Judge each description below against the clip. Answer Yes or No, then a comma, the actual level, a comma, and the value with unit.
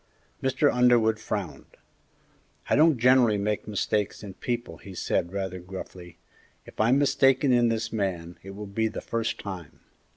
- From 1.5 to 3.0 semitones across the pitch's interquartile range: No, average, 4.1 semitones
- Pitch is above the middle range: No, low, 110 Hz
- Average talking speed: Yes, average, 155 wpm